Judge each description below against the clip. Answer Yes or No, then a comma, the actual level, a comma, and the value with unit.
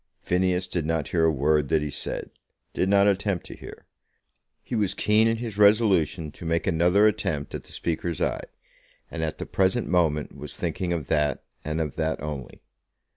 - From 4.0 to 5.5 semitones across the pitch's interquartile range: Yes, average, 4.3 semitones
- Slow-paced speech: No, average, 185 wpm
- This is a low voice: Yes, very low, 85 Hz